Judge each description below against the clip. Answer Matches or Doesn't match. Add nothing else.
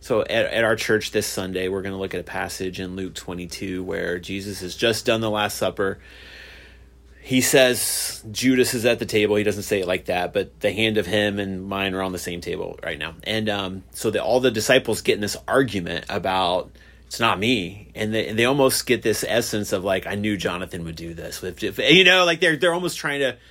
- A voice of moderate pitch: Doesn't match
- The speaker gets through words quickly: Matches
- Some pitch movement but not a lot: Matches